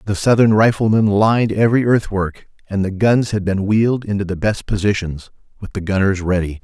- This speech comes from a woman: No, male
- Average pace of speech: Yes, average, 180 wpm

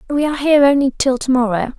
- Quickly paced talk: Yes, fast, 235 wpm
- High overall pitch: Yes, very high, 265 Hz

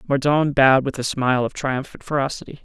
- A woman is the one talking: No, male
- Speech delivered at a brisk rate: No, average, 180 wpm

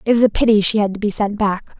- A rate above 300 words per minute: Yes, fast, 335 wpm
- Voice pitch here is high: Yes, high, 210 Hz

